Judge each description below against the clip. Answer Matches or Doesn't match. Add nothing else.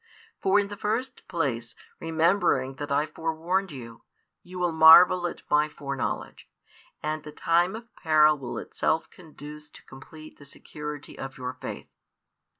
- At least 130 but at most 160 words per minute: Matches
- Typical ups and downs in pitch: Matches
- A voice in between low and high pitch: Matches